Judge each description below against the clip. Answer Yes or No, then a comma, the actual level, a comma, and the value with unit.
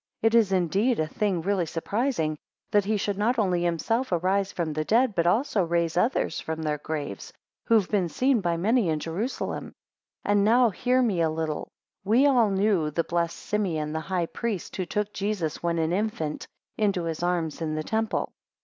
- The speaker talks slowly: No, average, 195 wpm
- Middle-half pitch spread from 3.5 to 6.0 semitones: Yes, average, 4.7 semitones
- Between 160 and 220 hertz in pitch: Yes, medium, 185 Hz